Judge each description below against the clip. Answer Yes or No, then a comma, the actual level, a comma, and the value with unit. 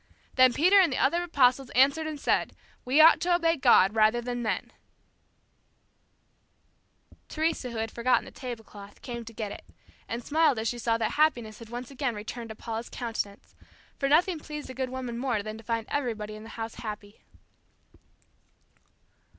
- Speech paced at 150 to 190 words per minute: Yes, average, 170 wpm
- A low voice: No, high, 245 Hz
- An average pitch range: Yes, average, 4.2 semitones